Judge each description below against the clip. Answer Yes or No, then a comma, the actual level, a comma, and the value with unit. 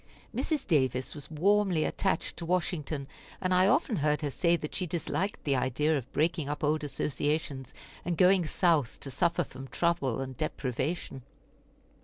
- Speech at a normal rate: Yes, average, 160 wpm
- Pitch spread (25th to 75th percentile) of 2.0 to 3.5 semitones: No, average, 4.2 semitones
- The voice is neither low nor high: Yes, medium, 155 Hz